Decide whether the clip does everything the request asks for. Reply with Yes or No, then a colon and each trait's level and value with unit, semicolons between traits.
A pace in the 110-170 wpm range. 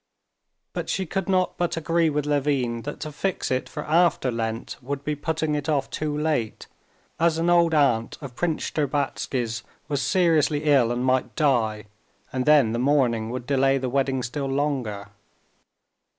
Yes: average, 165 wpm